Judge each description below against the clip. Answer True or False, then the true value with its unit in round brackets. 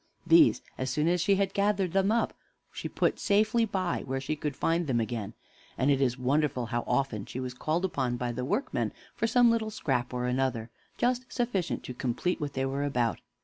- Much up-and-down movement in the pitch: True (7.9 semitones)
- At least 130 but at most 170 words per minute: False (205 wpm)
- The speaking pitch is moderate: True (145 Hz)